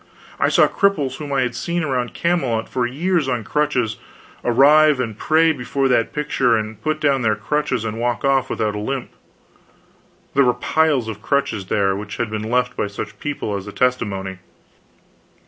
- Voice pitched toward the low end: Yes, low, 125 Hz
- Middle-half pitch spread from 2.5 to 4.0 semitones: No, average, 5.1 semitones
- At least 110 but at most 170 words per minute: No, average, 180 wpm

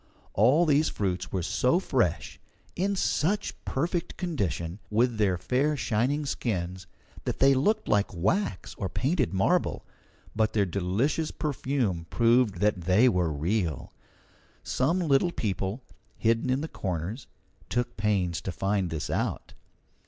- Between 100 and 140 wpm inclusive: Yes, slow, 135 wpm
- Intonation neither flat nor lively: No, wide, 6.7 semitones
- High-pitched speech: No, low, 110 Hz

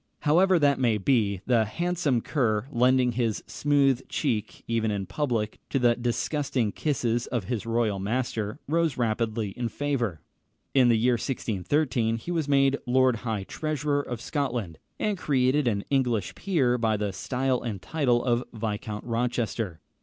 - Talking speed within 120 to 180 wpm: Yes, average, 155 wpm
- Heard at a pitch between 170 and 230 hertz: No, low, 120 Hz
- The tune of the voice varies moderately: Yes, average, 3.8 semitones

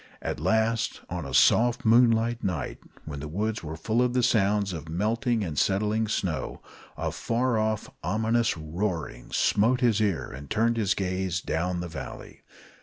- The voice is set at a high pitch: No, low, 105 Hz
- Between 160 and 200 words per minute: Yes, average, 170 wpm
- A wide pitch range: No, average, 4.8 semitones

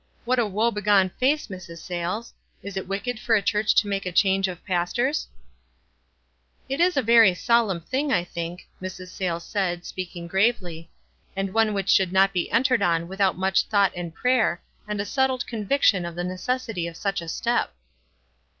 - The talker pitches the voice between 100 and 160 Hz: No, high, 195 Hz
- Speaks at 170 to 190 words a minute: Yes, average, 185 wpm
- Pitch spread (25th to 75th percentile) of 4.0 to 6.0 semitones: Yes, average, 4.5 semitones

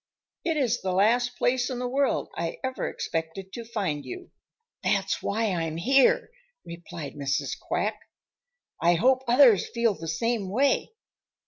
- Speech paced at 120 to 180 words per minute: Yes, average, 145 wpm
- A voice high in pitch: Yes, high, 230 Hz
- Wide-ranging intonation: Yes, wide, 6.9 semitones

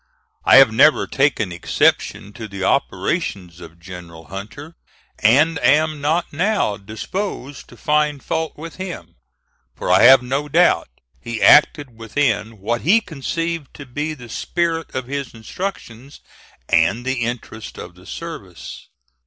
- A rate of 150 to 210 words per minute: No, average, 140 wpm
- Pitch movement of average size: No, wide, 6.3 semitones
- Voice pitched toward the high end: No, low, 130 Hz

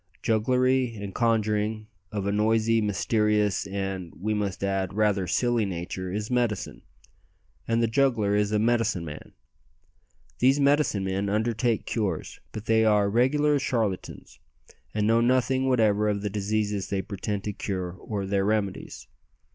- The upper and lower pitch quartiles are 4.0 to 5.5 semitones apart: No, narrow, 2.5 semitones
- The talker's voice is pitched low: Yes, low, 105 Hz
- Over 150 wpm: No, average, 145 wpm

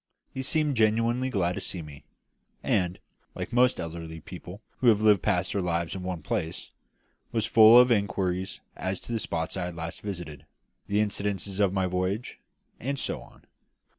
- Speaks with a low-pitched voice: Yes, very low, 95 Hz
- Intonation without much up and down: No, average, 4.0 semitones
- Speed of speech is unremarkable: Yes, average, 170 wpm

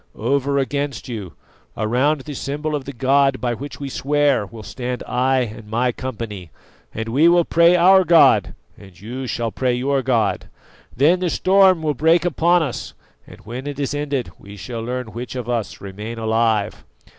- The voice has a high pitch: No, low, 130 Hz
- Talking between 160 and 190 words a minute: Yes, average, 180 wpm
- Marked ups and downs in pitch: No, average, 4.3 semitones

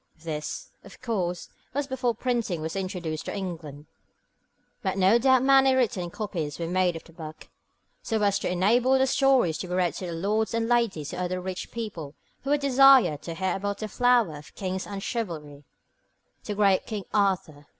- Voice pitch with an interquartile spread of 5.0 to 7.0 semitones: Yes, wide, 5.6 semitones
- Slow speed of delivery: No, average, 185 wpm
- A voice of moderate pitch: No, high, 195 Hz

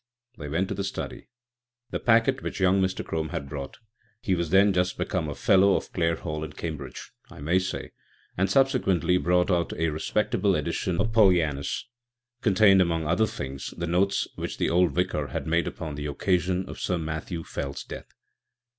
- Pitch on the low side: Yes, very low, 90 Hz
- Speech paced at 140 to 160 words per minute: No, average, 190 wpm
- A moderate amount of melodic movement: Yes, average, 3.5 semitones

